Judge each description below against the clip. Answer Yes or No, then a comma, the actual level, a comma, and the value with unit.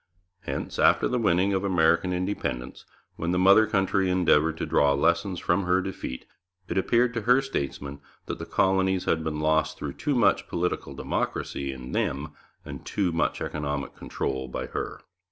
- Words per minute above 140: Yes, average, 170 wpm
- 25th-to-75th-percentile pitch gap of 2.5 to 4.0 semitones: No, average, 4.5 semitones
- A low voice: Yes, very low, 90 Hz